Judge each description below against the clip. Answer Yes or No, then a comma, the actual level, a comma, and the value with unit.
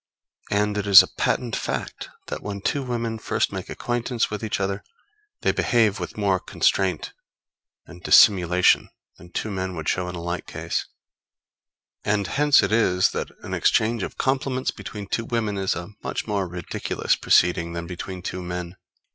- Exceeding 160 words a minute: Yes, average, 170 wpm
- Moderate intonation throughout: Yes, average, 4.0 semitones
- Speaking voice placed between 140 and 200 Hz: No, low, 100 Hz